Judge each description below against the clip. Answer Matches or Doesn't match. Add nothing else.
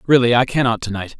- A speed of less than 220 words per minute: Doesn't match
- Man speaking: Matches